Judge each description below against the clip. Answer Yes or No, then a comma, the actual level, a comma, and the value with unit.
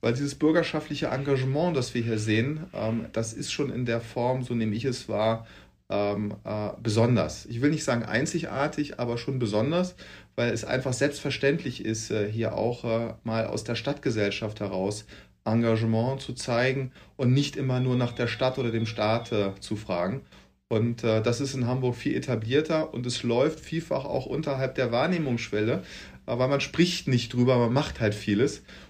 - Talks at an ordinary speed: Yes, average, 165 wpm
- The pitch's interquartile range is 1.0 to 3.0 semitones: No, average, 3.7 semitones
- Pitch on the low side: Yes, low, 120 Hz